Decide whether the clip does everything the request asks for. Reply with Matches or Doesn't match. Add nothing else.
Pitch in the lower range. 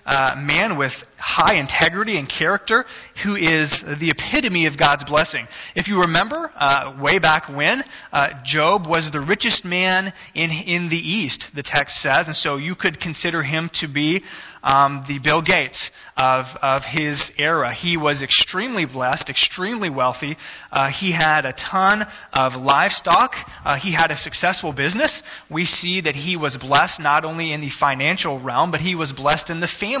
Doesn't match